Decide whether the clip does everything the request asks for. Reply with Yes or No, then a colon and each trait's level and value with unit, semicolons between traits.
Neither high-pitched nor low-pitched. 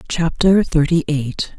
Yes: medium, 160 Hz